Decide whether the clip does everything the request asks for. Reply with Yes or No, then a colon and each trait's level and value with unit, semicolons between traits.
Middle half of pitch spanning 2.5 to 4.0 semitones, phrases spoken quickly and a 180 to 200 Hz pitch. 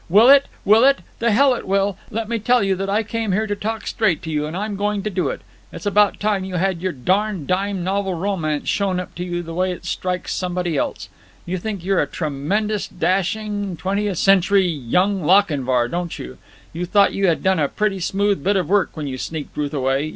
Yes: average, 3.1 semitones; fast, 225 wpm; high, 190 Hz